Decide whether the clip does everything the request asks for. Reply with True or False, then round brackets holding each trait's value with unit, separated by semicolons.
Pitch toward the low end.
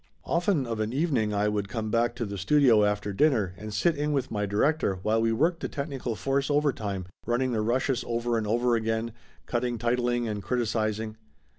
True (115 Hz)